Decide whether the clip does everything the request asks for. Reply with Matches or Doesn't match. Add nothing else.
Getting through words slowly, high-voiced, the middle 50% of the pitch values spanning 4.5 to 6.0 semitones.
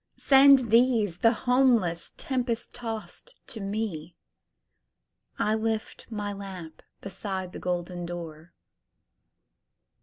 Matches